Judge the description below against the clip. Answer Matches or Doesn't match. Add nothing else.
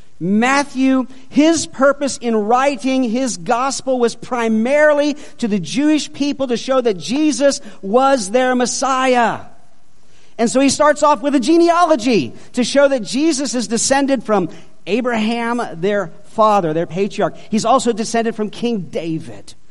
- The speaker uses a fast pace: Doesn't match